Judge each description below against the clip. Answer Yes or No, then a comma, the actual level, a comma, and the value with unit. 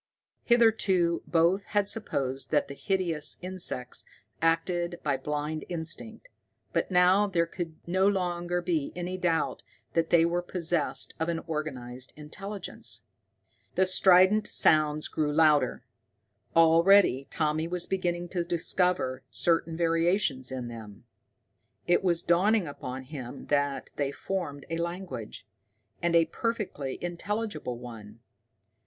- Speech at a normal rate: No, slow, 125 wpm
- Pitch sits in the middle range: Yes, medium, 170 Hz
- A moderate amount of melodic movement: Yes, average, 3.6 semitones